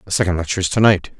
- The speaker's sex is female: No, male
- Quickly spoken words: Yes, fast, 250 wpm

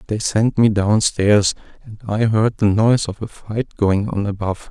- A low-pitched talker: Yes, low, 105 Hz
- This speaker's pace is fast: No, average, 190 wpm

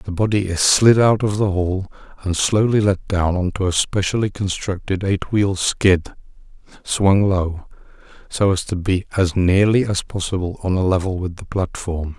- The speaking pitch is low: Yes, very low, 95 Hz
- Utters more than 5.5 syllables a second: No, 4.5 syllables/s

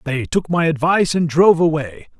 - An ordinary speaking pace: Yes, average, 190 wpm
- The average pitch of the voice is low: No, medium, 155 Hz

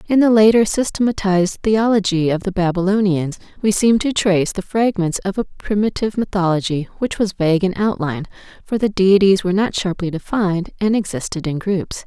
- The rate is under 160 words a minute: No, average, 170 wpm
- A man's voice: No, female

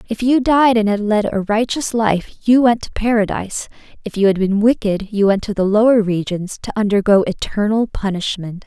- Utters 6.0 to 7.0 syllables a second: No, 5.2 syllables/s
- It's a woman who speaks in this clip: Yes, female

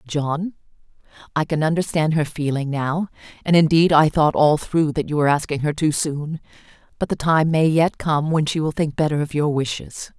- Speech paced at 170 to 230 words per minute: Yes, average, 200 wpm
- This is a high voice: No, medium, 155 Hz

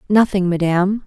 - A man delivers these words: No, female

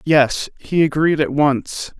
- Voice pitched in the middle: Yes, medium, 150 Hz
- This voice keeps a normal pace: Yes, average, 150 wpm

